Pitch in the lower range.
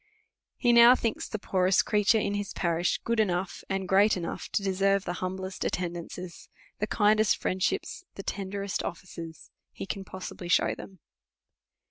No: high, 195 Hz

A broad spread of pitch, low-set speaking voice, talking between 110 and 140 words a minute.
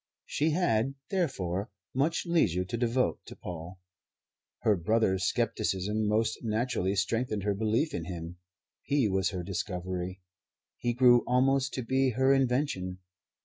Yes: wide, 6.0 semitones; low, 110 Hz; slow, 135 wpm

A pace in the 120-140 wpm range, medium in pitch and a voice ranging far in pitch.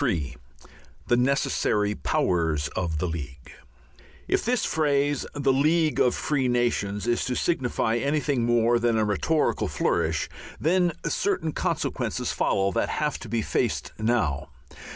No: slow, 135 wpm; low, 120 Hz; wide, 6.3 semitones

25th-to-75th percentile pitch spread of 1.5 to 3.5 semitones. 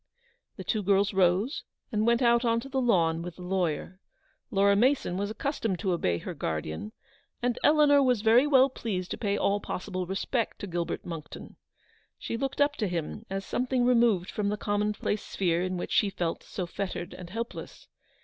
No: average, 4.8 semitones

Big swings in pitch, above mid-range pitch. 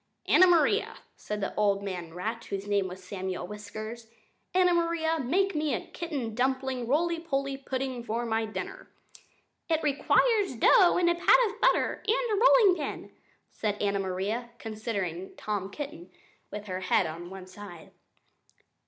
Yes: wide, 8.5 semitones; high, 230 Hz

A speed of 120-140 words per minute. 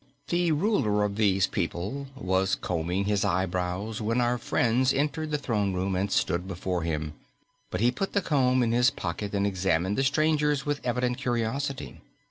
No: average, 170 wpm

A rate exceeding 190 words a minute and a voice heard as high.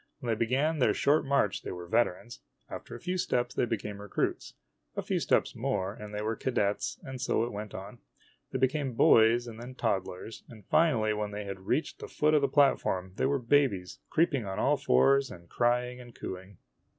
No: average, 200 wpm; low, 115 Hz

